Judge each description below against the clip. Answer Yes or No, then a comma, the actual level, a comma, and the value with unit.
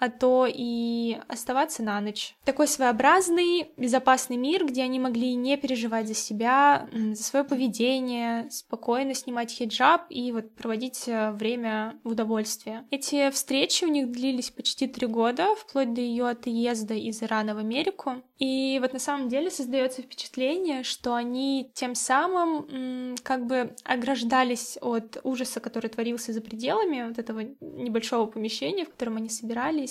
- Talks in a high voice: Yes, very high, 250 Hz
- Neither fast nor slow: Yes, average, 145 wpm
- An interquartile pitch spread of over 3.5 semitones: No, narrow, 2.6 semitones